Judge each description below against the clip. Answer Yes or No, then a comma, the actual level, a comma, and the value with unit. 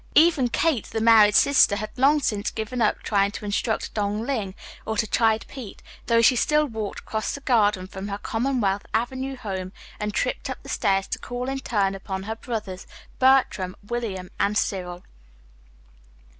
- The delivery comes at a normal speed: Yes, average, 170 wpm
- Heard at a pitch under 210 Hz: No, high, 220 Hz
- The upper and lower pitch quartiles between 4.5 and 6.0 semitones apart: No, average, 3.8 semitones